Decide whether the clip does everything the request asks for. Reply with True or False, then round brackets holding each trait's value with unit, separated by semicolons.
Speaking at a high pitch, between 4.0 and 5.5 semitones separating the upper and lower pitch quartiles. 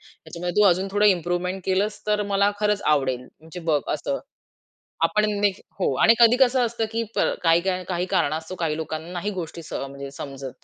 False (180 Hz; 4.5 semitones)